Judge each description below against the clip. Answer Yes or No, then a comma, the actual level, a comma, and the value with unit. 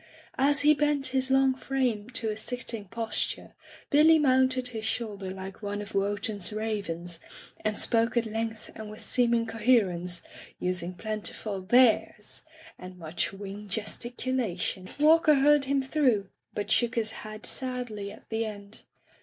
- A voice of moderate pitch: No, high, 220 Hz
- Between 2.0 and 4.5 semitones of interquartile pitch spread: Yes, average, 4.1 semitones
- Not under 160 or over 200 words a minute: No, average, 145 wpm